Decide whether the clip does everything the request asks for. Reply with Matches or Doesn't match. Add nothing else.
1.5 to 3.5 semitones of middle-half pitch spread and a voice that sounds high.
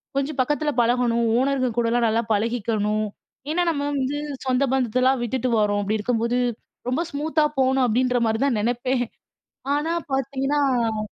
Matches